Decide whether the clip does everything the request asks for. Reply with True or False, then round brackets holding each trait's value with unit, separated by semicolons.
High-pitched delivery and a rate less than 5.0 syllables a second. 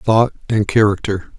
False (105 Hz; 4.3 syllables/s)